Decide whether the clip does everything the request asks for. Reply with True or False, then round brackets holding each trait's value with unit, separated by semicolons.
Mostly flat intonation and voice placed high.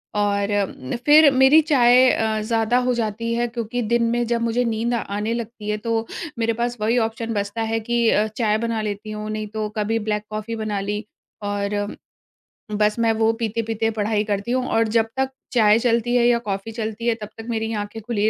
True (1.8 semitones; 225 Hz)